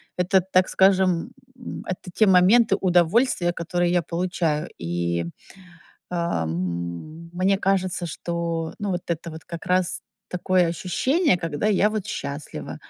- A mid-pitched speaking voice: Yes, medium, 175 Hz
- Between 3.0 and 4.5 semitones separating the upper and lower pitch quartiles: No, narrow, 2.4 semitones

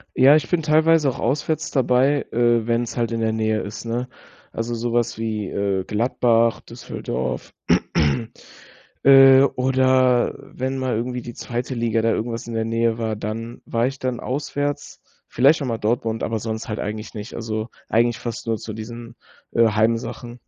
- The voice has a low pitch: Yes, low, 120 Hz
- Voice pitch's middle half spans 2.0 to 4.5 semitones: Yes, narrow, 2.5 semitones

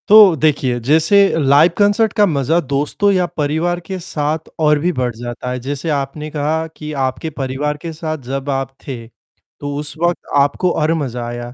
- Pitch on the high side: No, medium, 150 Hz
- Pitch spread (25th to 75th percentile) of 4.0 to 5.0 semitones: No, average, 3.4 semitones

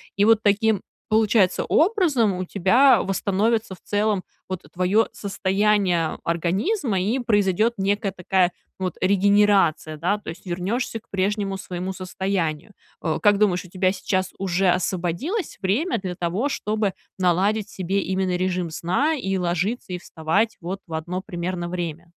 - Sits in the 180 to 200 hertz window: Yes, high, 190 Hz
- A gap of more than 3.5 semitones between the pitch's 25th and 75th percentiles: No, average, 2.8 semitones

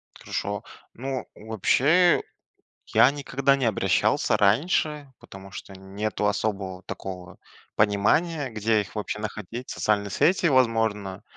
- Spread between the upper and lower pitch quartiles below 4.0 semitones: No, average, 5.3 semitones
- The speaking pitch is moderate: No, low, 110 Hz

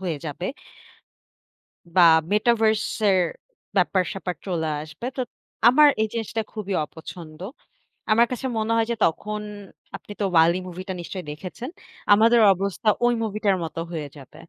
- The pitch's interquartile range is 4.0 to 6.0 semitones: Yes, average, 4.4 semitones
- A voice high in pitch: Yes, high, 195 Hz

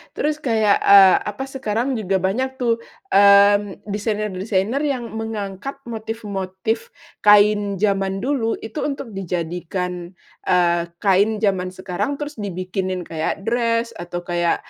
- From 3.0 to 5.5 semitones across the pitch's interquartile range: Yes, average, 3.4 semitones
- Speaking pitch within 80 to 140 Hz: No, high, 205 Hz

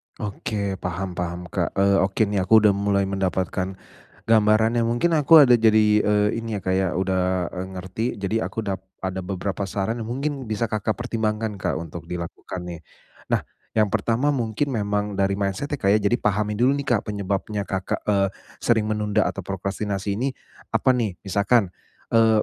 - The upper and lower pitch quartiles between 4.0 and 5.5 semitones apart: No, average, 2.7 semitones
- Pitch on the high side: No, low, 105 Hz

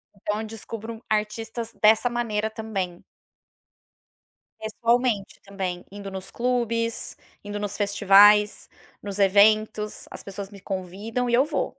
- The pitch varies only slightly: Yes, narrow, 2.3 semitones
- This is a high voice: Yes, high, 210 Hz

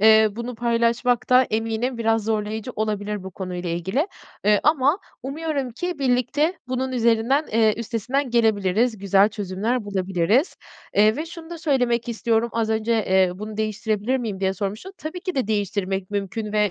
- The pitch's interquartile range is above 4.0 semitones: No, average, 3.5 semitones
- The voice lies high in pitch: Yes, high, 225 Hz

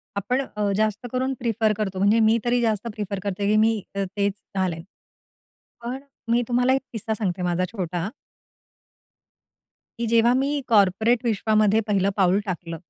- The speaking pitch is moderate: No, high, 215 Hz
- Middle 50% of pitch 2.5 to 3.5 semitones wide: Yes, average, 3.0 semitones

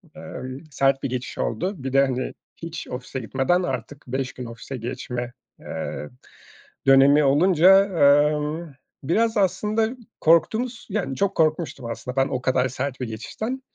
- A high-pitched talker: No, medium, 140 Hz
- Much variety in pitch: Yes, wide, 5.8 semitones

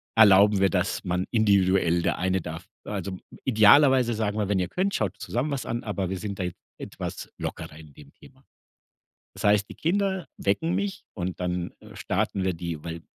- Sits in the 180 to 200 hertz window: No, low, 100 Hz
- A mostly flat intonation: No, average, 3.9 semitones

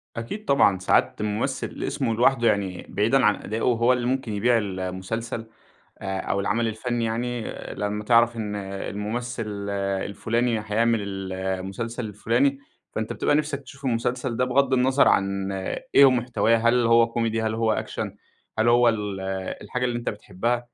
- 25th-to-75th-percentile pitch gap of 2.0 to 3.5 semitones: Yes, average, 2.9 semitones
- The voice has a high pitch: No, low, 115 Hz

